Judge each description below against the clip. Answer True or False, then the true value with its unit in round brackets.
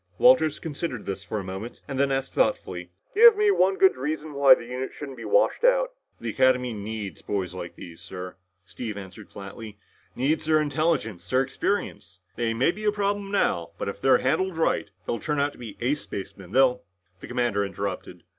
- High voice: False (130 Hz)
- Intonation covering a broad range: True (7.7 semitones)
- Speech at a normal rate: True (195 wpm)